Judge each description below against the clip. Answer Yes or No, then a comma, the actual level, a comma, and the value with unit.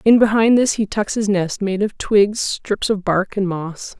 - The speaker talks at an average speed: No, fast, 225 wpm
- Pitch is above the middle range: Yes, high, 200 Hz